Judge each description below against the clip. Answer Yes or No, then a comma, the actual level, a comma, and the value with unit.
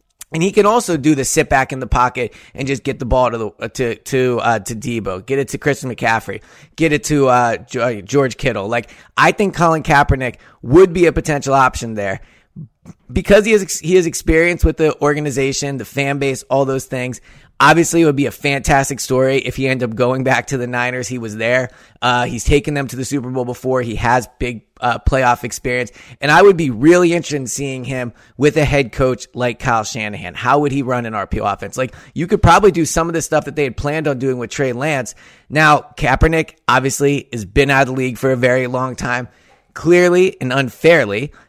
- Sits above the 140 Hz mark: No, low, 135 Hz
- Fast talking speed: Yes, fast, 220 wpm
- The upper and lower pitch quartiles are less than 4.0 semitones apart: Yes, average, 3.2 semitones